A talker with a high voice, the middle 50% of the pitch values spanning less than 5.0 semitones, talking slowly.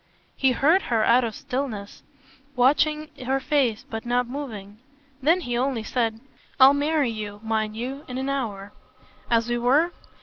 No: very high, 250 Hz; average, 3.8 semitones; average, 160 wpm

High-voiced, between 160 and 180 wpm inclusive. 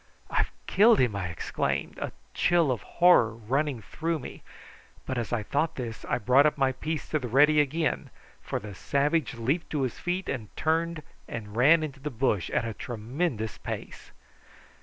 No: low, 135 Hz; average, 175 wpm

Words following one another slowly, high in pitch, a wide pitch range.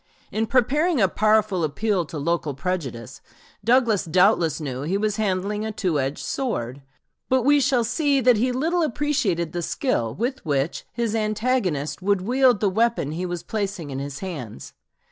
No: average, 165 wpm; high, 205 Hz; wide, 6.9 semitones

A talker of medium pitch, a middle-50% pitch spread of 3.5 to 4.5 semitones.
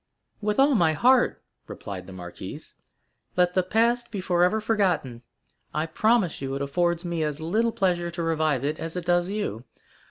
No: medium, 175 Hz; average, 5.2 semitones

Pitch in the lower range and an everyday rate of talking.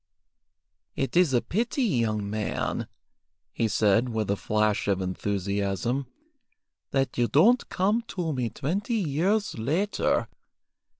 No: low, 125 Hz; slow, 120 wpm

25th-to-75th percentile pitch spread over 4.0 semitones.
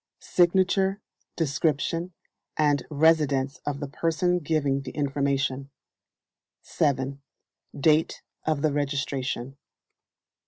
No: average, 2.8 semitones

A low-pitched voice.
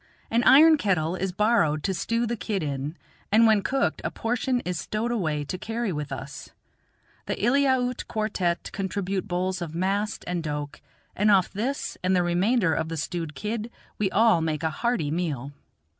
No: high, 190 Hz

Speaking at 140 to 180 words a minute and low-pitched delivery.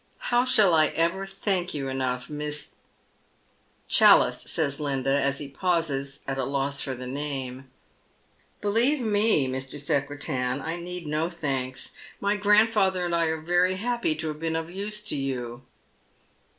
No: average, 165 wpm; medium, 155 Hz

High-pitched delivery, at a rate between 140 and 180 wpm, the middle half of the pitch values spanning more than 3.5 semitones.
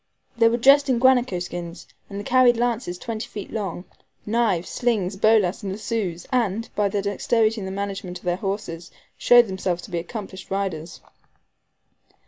Yes: high, 205 Hz; average, 160 wpm; average, 4.0 semitones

